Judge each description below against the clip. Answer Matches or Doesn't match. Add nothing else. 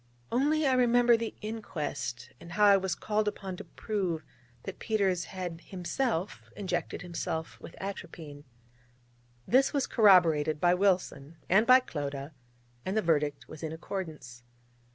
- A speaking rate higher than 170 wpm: Doesn't match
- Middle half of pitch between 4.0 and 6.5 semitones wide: Matches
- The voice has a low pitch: Doesn't match